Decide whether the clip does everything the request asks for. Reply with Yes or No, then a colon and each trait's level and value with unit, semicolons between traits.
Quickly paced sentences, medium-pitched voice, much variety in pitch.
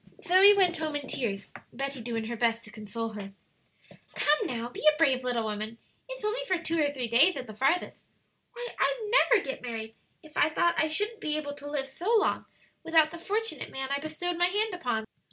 No: fast, 210 wpm; very high, 290 Hz; wide, 6.9 semitones